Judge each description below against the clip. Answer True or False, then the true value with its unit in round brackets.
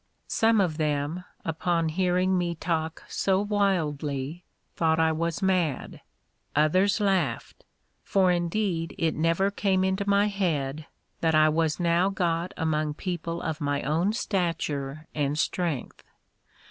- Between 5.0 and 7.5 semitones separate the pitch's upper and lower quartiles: False (3.4 semitones)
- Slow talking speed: True (130 wpm)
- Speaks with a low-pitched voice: False (170 Hz)